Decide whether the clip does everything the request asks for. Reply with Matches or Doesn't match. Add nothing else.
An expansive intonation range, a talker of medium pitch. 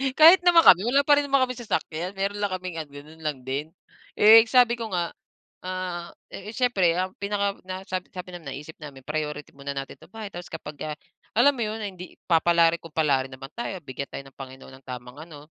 Matches